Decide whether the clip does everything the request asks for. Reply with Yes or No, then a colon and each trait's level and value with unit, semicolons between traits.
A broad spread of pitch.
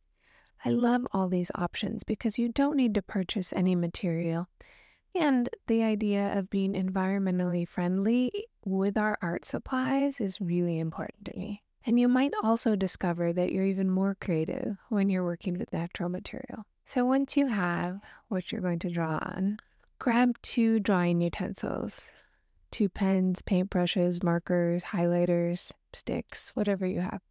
No: average, 3.8 semitones